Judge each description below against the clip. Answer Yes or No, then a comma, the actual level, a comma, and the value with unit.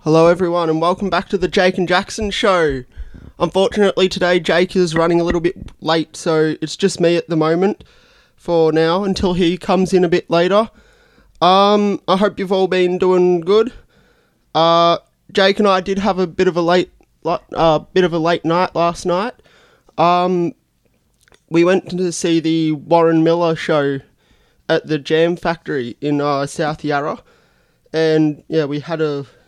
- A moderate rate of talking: Yes, average, 175 wpm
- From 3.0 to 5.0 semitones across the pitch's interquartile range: No, narrow, 2.5 semitones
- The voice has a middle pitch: Yes, medium, 175 Hz